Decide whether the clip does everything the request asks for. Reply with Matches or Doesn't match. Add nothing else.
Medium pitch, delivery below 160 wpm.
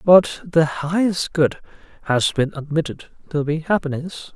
Matches